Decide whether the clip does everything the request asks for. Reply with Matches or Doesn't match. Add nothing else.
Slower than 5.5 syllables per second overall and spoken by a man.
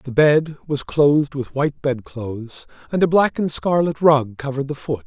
Matches